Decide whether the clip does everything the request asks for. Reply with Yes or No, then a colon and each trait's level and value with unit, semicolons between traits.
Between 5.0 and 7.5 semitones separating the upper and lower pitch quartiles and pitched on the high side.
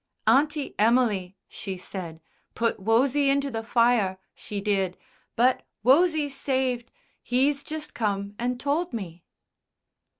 Yes: wide, 5.6 semitones; high, 240 Hz